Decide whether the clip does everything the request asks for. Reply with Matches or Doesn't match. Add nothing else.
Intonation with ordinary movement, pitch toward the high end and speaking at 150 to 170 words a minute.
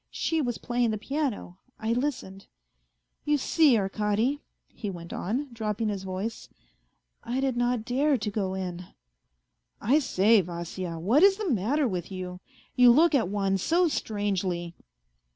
Doesn't match